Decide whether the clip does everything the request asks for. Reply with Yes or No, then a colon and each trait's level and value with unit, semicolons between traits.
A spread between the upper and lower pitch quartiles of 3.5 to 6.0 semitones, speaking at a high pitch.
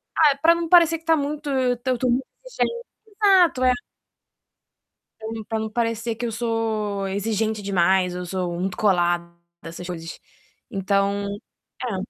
Yes: wide, 5.4 semitones; high, 220 Hz